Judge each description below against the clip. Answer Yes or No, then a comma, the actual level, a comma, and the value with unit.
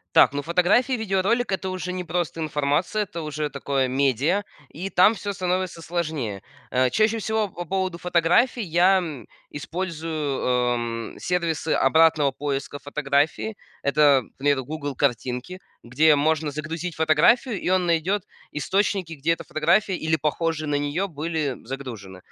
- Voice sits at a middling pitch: Yes, medium, 160 Hz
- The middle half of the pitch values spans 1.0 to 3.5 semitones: No, average, 4.2 semitones